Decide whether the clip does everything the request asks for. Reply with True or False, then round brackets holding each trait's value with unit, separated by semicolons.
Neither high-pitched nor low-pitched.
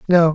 True (170 Hz)